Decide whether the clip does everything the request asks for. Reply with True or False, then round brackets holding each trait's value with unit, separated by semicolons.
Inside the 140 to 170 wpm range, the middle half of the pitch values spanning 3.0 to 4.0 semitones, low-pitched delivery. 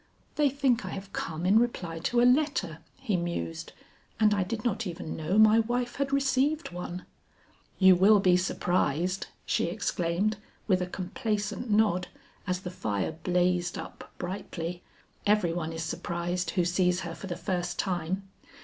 False (160 wpm; 3.7 semitones; 185 Hz)